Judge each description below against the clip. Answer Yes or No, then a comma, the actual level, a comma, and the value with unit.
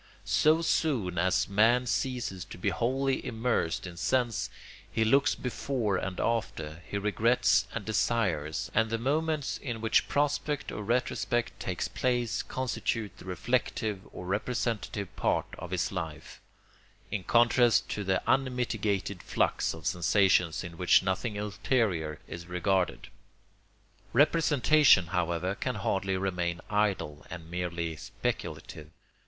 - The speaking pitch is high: No, low, 105 Hz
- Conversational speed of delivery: No, slow, 125 wpm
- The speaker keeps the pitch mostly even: No, average, 5.3 semitones